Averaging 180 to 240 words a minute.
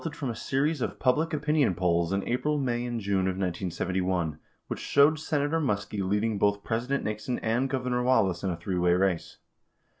Yes: average, 190 wpm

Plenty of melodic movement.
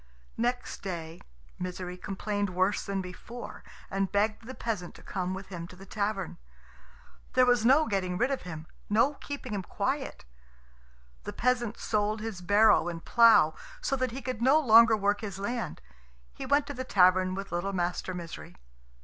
No: average, 4.6 semitones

